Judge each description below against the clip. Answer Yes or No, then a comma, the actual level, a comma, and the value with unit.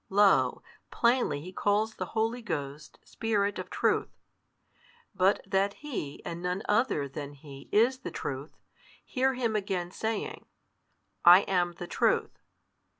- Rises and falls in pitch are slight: No, wide, 5.6 semitones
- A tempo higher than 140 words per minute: No, slow, 135 wpm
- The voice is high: Yes, high, 195 Hz